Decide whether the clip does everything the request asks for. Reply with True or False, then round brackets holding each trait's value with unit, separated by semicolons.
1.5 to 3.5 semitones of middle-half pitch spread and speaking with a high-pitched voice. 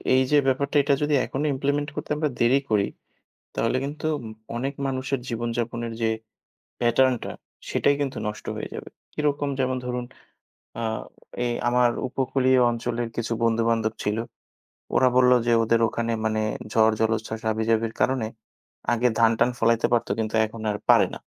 False (2.7 semitones; 120 Hz)